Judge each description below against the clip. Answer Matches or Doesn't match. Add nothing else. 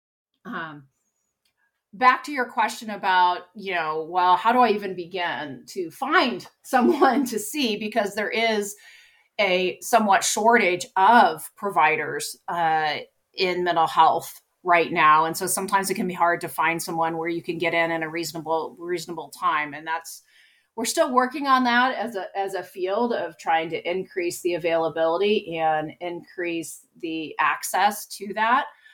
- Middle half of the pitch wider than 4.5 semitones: Matches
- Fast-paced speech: Doesn't match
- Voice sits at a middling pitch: Matches